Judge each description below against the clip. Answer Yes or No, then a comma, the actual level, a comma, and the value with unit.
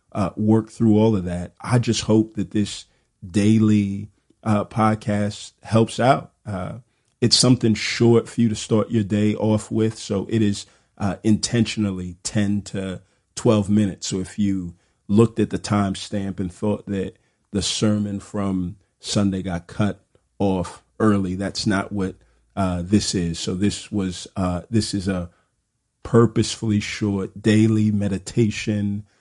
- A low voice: Yes, low, 105 Hz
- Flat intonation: Yes, narrow, 2.1 semitones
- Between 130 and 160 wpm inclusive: Yes, average, 150 wpm